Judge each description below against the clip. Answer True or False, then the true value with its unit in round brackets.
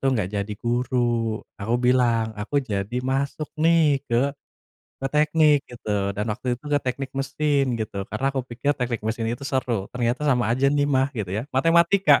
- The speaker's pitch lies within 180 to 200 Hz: False (125 Hz)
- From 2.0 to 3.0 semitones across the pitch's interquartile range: False (3.7 semitones)